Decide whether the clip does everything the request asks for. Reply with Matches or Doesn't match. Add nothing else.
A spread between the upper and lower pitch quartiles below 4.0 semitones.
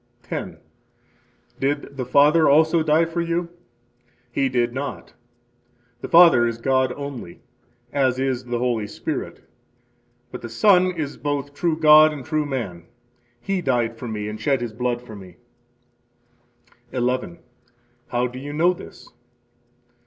Doesn't match